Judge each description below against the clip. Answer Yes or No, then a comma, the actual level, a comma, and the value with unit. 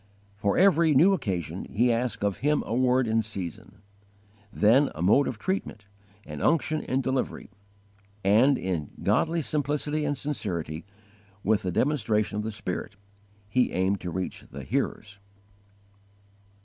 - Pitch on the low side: Yes, low, 110 Hz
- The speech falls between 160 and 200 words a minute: No, average, 145 wpm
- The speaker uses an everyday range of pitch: No, wide, 6.6 semitones